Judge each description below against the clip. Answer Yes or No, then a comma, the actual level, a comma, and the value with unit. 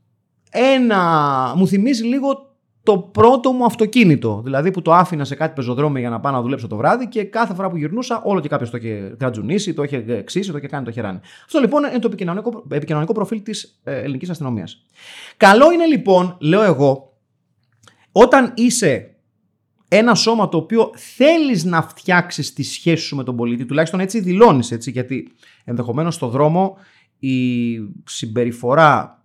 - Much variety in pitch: Yes, wide, 8.7 semitones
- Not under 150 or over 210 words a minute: Yes, average, 165 wpm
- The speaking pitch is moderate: Yes, medium, 165 Hz